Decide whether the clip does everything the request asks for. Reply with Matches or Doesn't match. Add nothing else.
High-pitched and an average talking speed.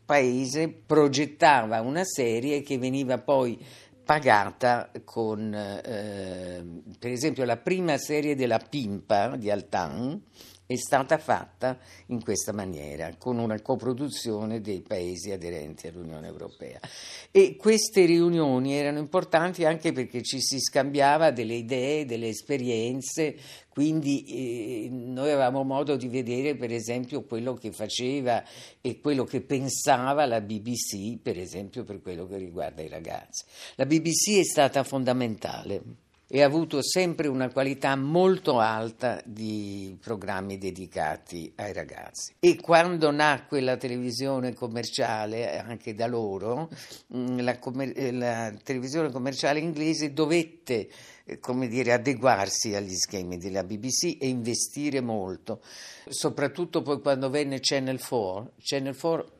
Doesn't match